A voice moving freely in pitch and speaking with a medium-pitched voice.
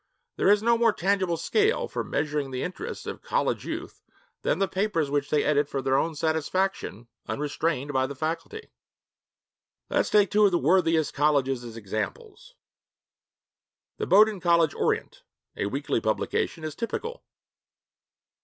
Yes: wide, 6.1 semitones; medium, 160 Hz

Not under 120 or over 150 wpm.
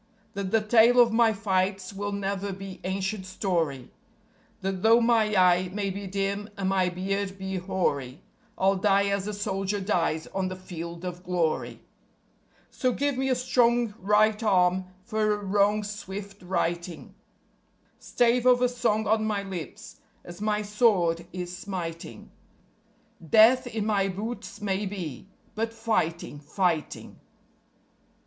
Yes: average, 140 wpm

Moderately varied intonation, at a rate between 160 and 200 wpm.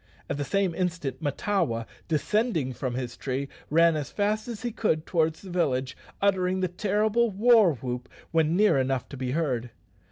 No: wide, 7.0 semitones; average, 170 wpm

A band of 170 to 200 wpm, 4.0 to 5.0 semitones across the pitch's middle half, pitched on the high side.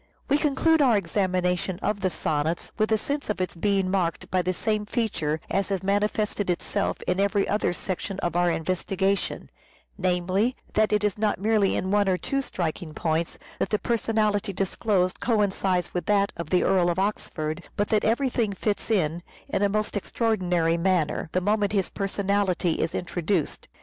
No: average, 175 wpm; average, 2.9 semitones; high, 195 Hz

